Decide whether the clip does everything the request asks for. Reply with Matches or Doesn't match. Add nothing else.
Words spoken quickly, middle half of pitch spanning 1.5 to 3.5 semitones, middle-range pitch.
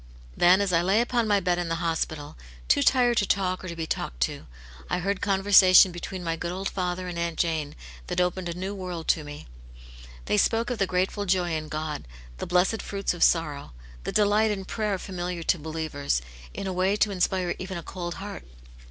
Matches